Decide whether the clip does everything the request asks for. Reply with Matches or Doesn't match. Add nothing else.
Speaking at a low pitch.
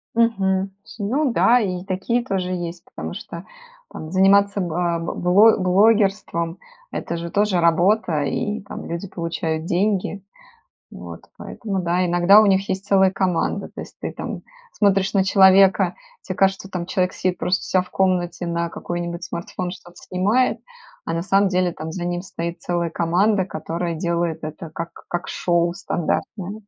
Doesn't match